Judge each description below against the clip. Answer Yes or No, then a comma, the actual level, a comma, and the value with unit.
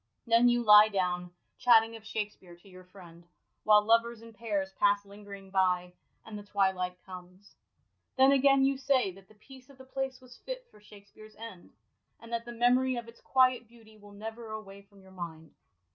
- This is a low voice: No, high, 215 Hz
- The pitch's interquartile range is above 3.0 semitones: Yes, average, 3.6 semitones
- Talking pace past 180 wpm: Yes, average, 190 wpm